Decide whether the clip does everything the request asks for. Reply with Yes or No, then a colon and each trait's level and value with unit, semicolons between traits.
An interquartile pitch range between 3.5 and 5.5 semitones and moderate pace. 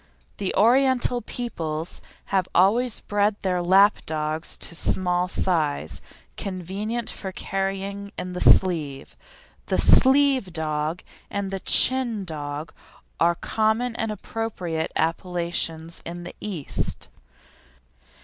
No: average, 4.3 semitones; slow, 110 wpm